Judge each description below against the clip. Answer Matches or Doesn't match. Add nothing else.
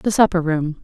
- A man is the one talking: Doesn't match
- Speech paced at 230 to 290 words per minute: Doesn't match